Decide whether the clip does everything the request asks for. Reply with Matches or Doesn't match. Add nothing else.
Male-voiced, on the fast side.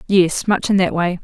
Doesn't match